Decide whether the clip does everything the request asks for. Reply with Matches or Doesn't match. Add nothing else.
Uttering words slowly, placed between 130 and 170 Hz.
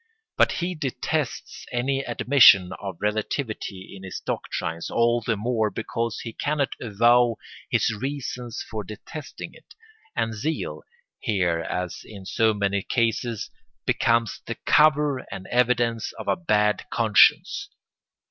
Doesn't match